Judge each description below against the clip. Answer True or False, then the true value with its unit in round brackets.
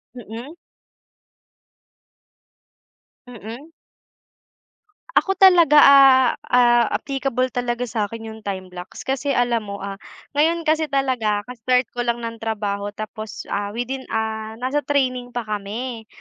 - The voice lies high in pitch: True (240 Hz)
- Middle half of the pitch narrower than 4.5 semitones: True (3.5 semitones)